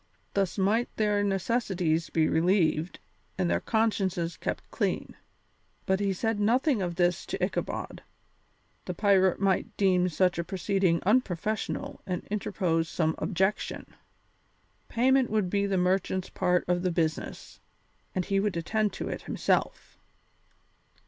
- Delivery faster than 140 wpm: No, slow, 135 wpm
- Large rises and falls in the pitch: No, average, 2.8 semitones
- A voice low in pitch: No, high, 190 Hz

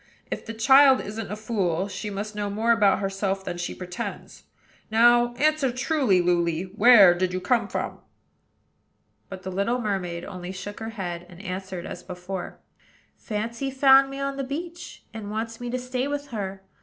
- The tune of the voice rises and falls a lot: No, average, 4.8 semitones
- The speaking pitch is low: No, high, 210 Hz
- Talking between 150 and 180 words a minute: Yes, average, 175 wpm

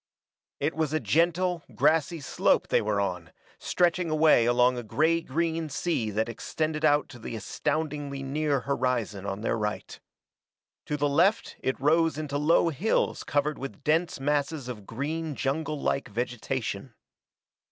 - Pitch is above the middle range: No, medium, 145 Hz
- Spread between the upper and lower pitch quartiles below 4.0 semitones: No, average, 4.4 semitones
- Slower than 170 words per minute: Yes, average, 145 wpm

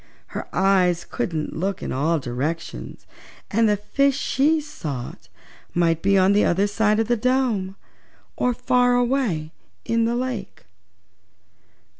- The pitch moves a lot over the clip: Yes, wide, 6.4 semitones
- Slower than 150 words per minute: Yes, slow, 135 wpm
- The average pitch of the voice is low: No, high, 205 Hz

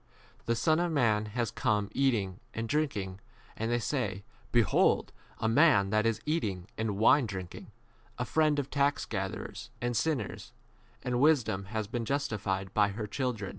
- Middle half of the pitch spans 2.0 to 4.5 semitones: No, average, 5.3 semitones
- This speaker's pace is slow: No, average, 160 wpm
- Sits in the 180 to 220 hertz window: No, low, 115 Hz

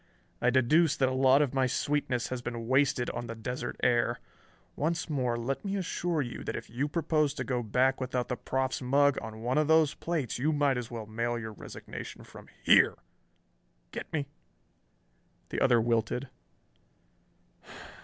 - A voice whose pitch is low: Yes, low, 130 Hz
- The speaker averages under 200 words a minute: Yes, average, 170 wpm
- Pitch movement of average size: Yes, average, 3.3 semitones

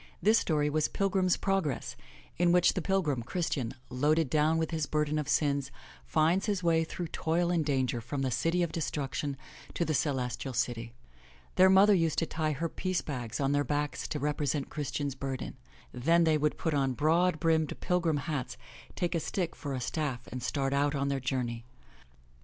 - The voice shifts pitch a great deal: No, average, 3.5 semitones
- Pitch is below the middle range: No, medium, 150 Hz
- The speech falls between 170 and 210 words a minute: Yes, average, 190 wpm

